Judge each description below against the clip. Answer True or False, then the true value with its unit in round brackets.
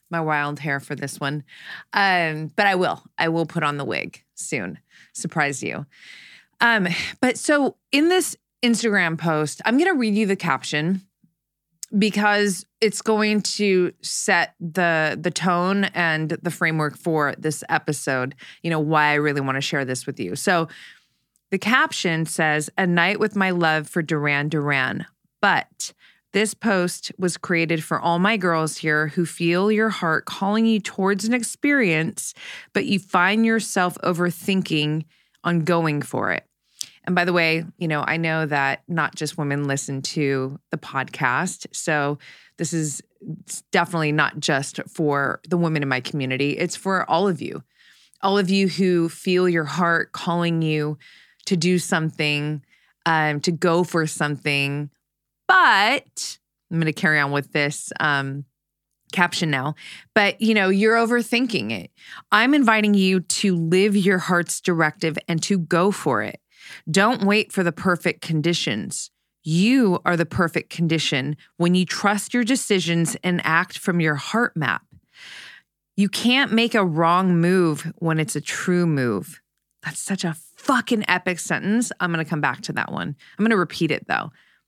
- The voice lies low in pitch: False (170 Hz)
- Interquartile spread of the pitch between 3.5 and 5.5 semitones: True (4.2 semitones)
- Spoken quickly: False (165 wpm)